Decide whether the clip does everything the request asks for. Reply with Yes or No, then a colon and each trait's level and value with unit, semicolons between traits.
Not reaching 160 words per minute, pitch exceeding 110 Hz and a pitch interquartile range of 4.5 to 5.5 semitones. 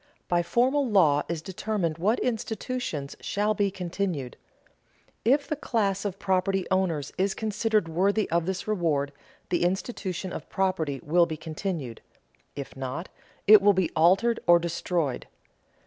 No: average, 140 wpm; medium, 185 Hz; average, 4.0 semitones